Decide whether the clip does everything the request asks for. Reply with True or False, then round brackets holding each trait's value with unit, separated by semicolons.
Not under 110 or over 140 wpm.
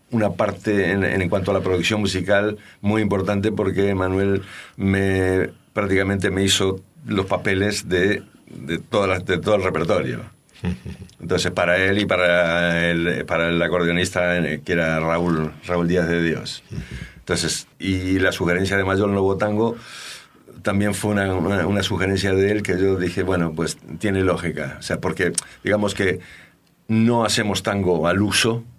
False (160 wpm)